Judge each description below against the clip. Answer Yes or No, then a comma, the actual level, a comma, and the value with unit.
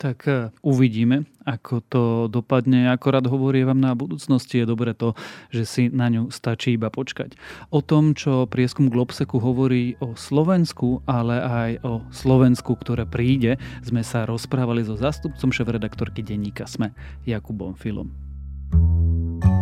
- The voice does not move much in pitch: Yes, narrow, 2.3 semitones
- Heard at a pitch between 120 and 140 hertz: Yes, low, 125 Hz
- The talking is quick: No, average, 135 wpm